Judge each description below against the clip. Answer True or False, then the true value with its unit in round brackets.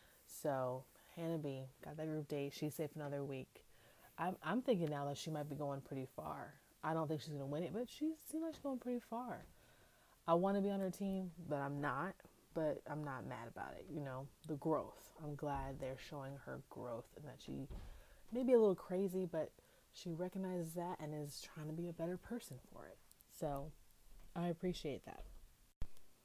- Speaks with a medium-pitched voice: True (155 Hz)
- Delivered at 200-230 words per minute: True (205 wpm)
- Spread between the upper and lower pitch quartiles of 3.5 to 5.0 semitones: True (4.6 semitones)